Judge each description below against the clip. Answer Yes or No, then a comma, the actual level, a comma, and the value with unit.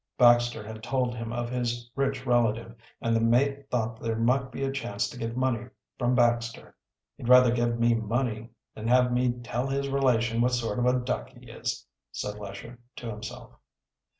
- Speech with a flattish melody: Yes, narrow, 1.7 semitones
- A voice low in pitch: Yes, low, 120 Hz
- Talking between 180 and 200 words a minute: Yes, average, 185 wpm